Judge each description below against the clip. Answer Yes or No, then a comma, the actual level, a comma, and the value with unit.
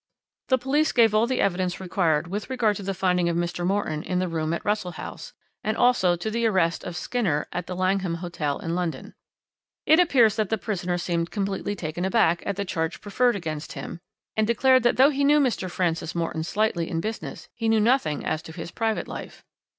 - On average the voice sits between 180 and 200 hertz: Yes, high, 190 Hz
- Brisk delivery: Yes, fast, 210 wpm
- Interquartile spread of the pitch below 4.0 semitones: No, average, 4.5 semitones